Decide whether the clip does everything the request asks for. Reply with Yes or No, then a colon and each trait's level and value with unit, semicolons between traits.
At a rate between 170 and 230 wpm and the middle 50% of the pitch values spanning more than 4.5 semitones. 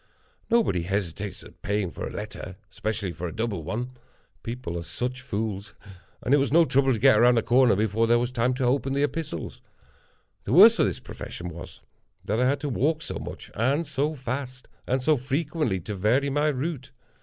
Yes: average, 190 wpm; average, 5.0 semitones